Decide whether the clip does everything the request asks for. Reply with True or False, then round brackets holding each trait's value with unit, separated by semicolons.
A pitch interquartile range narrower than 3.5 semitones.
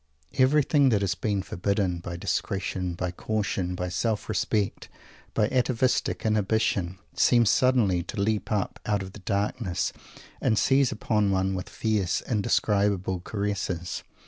True (3.0 semitones)